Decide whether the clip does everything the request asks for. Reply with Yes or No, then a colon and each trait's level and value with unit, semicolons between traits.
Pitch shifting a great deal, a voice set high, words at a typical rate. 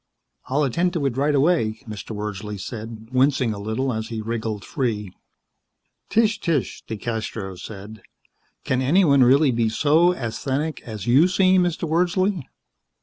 No: wide, 6.1 semitones; low, 130 Hz; average, 145 wpm